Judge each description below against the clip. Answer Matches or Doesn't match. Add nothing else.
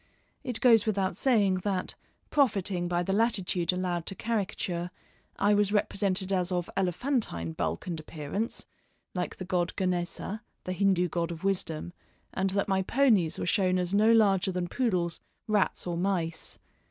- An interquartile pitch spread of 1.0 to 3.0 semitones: Matches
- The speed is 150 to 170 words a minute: Matches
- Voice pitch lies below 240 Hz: Matches